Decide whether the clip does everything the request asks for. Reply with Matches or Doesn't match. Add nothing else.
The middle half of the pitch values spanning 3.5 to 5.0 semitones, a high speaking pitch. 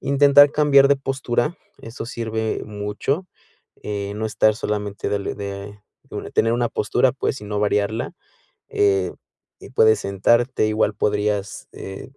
Doesn't match